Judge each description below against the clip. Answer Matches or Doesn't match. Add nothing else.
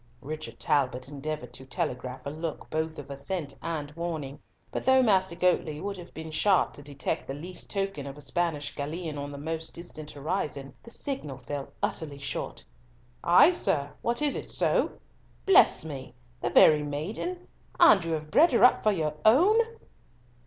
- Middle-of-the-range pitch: Matches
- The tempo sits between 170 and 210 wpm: Matches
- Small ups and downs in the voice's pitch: Doesn't match